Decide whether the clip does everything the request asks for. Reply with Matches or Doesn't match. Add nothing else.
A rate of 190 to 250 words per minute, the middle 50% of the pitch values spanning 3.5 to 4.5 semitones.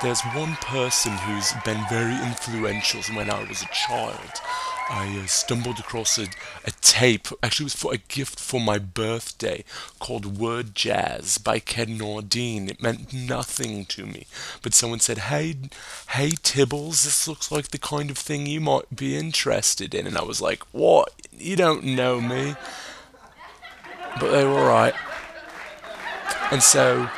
Doesn't match